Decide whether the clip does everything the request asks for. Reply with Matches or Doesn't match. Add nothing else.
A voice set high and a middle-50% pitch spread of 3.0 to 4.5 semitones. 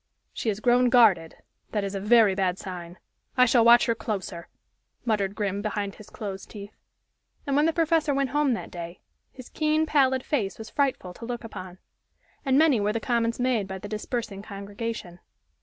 Matches